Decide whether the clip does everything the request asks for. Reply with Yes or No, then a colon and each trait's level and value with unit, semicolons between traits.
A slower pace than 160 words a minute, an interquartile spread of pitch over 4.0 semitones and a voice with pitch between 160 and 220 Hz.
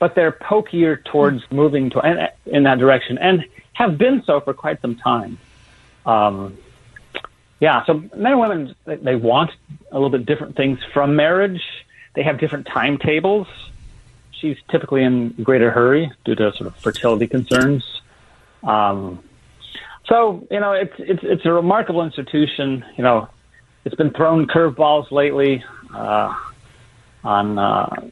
No: average, 145 wpm; average, 5.3 semitones; medium, 140 Hz